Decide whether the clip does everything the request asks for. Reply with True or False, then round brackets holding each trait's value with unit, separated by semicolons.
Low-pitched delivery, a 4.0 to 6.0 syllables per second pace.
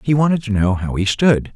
True (115 Hz; 5.5 syllables/s)